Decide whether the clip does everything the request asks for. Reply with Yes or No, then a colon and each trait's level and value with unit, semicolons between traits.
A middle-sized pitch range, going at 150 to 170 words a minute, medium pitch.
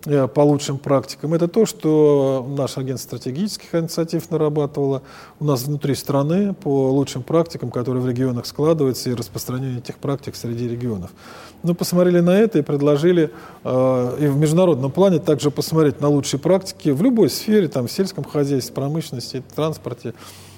Yes: average, 3.8 semitones; average, 155 wpm; medium, 145 Hz